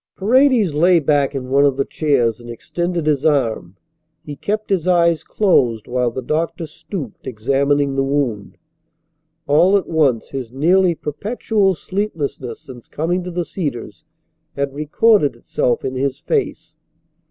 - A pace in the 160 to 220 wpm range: No, average, 145 wpm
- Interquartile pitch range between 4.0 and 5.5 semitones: Yes, average, 5.1 semitones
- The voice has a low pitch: No, medium, 145 Hz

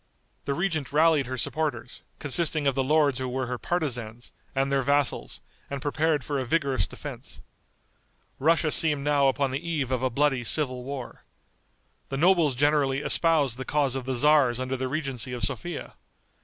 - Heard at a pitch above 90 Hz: Yes, medium, 140 Hz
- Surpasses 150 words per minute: Yes, average, 170 wpm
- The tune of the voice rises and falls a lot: No, average, 2.7 semitones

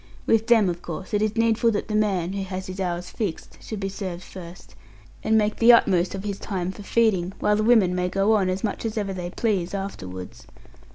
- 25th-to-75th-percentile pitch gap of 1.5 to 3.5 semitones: Yes, average, 3.0 semitones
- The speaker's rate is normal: No, fast, 225 wpm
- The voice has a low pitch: No, high, 195 Hz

